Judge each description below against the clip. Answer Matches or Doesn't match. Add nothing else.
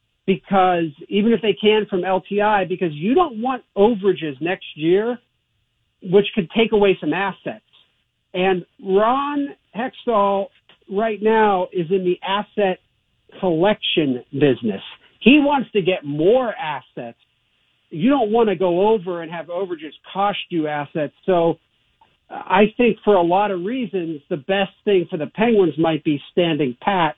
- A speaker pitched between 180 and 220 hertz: Matches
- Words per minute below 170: Matches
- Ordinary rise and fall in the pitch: Matches